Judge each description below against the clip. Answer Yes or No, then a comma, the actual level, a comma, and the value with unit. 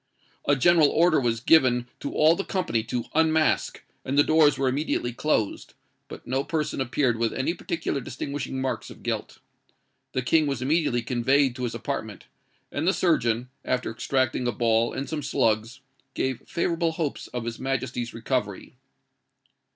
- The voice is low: Yes, low, 130 Hz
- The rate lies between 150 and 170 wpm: Yes, average, 160 wpm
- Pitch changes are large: No, average, 4.2 semitones